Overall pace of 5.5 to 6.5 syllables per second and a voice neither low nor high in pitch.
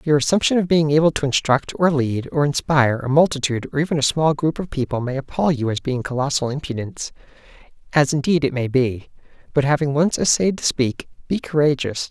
Yes: 5.9 syllables/s; medium, 145 Hz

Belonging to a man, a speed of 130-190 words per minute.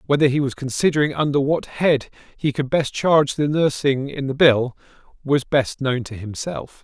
Yes: male; average, 185 wpm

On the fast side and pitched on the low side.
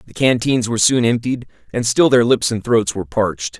Yes: fast, 215 wpm; low, 115 Hz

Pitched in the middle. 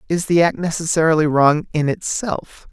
Yes: medium, 165 Hz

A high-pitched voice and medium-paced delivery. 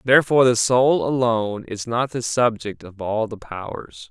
No: low, 115 Hz; average, 175 wpm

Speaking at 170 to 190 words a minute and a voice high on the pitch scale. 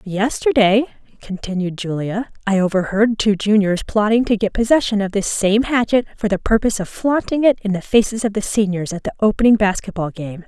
Yes: average, 185 wpm; high, 210 Hz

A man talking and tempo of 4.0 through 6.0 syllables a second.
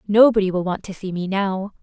No: female; 5.5 syllables/s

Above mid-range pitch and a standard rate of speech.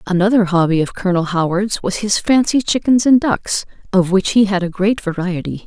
Yes: high, 195 Hz; average, 190 wpm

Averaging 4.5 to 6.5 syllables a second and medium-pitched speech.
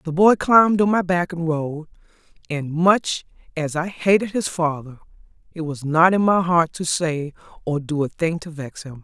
Yes: 4.6 syllables/s; medium, 165 Hz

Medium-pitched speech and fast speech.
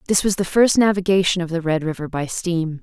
Yes: medium, 175 Hz; fast, 235 wpm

